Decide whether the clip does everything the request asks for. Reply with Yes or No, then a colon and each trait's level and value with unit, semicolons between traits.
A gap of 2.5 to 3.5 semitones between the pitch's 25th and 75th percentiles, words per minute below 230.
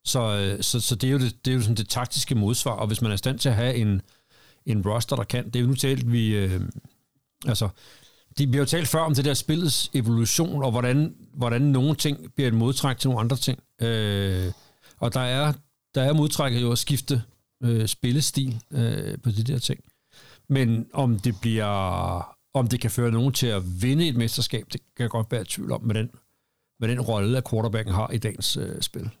Yes: average, 3.1 semitones; average, 220 wpm